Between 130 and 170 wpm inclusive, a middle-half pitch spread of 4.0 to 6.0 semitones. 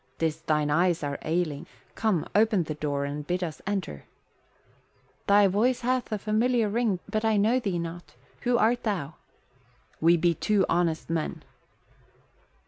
Yes: average, 150 wpm; average, 5.2 semitones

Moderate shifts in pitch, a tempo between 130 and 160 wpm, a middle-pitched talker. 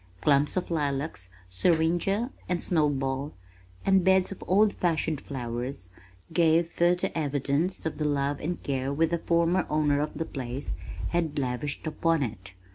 Yes: average, 3.8 semitones; average, 150 wpm; medium, 155 Hz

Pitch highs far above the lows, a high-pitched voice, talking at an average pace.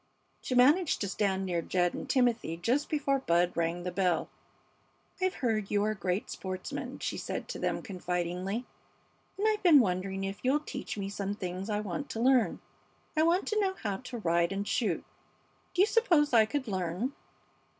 Yes: wide, 6.7 semitones; high, 205 Hz; average, 180 wpm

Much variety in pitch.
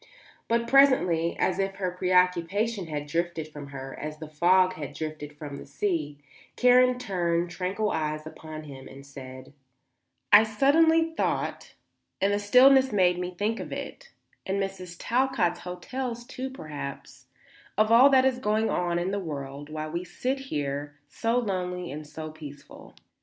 Yes: wide, 6.9 semitones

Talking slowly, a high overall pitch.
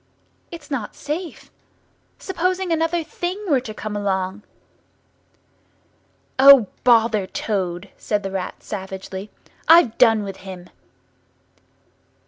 Yes: slow, 105 wpm; high, 220 Hz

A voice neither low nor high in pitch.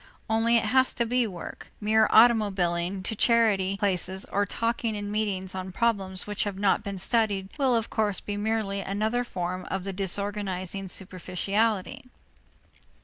No: high, 205 Hz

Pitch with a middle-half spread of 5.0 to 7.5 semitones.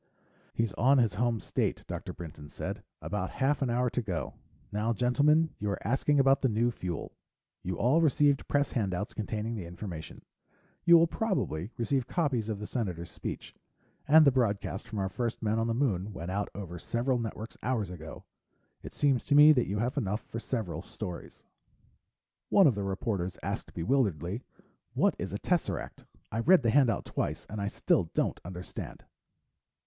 Yes: wide, 5.5 semitones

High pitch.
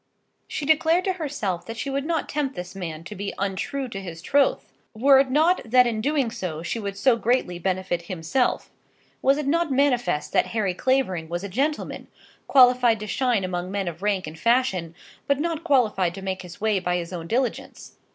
Yes: high, 220 Hz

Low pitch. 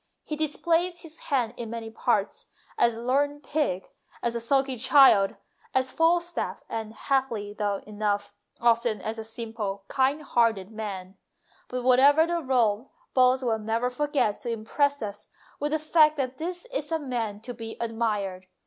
No: high, 245 Hz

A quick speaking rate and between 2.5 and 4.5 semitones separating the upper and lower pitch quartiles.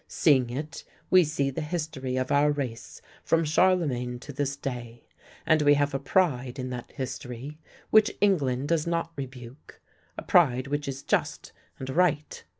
No: average, 160 wpm; average, 3.4 semitones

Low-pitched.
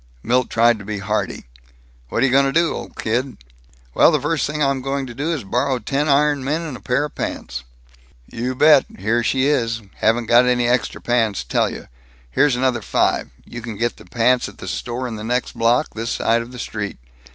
Yes: low, 125 Hz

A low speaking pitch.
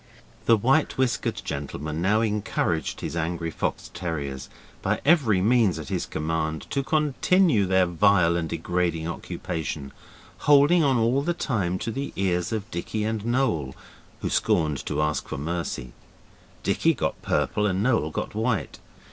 Yes: very low, 95 Hz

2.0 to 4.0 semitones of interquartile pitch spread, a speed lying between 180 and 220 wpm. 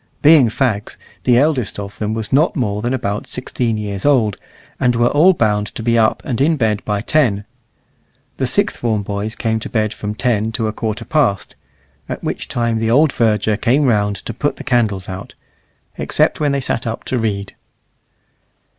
Yes: average, 3.5 semitones; average, 190 wpm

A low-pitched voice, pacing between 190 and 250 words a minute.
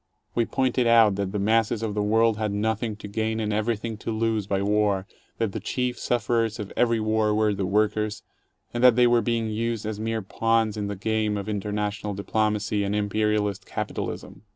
Yes: low, 110 Hz; average, 195 wpm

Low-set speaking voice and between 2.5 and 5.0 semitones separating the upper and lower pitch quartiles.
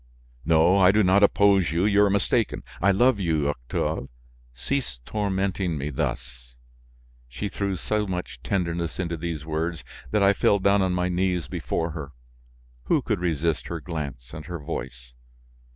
Yes: very low, 90 Hz; average, 4.3 semitones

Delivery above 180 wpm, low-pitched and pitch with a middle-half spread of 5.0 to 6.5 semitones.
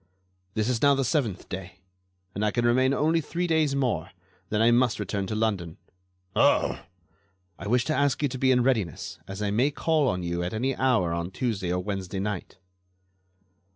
Yes: average, 190 wpm; low, 115 Hz; wide, 5.5 semitones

